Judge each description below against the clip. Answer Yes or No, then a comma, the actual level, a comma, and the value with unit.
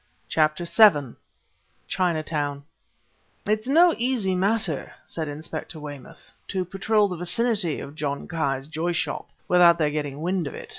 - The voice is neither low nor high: Yes, medium, 170 Hz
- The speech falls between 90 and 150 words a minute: Yes, average, 140 wpm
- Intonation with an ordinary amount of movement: Yes, average, 4.5 semitones